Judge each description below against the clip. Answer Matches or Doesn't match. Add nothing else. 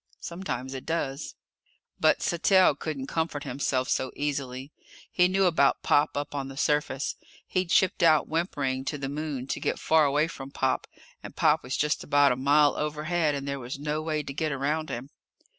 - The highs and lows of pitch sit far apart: Doesn't match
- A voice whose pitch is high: Doesn't match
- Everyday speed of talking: Matches